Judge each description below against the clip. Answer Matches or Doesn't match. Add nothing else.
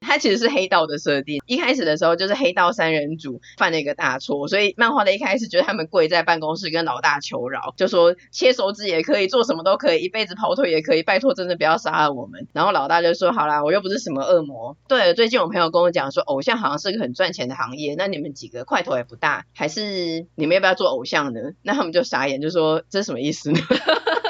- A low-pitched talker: Doesn't match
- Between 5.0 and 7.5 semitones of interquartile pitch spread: Matches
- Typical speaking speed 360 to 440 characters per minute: Matches